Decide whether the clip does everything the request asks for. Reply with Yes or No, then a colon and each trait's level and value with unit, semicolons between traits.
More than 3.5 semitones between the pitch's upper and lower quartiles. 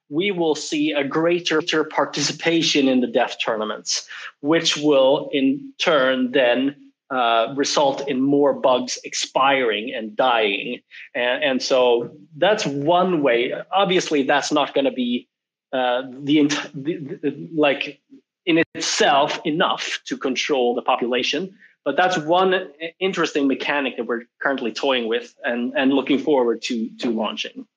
Yes: average, 5.2 semitones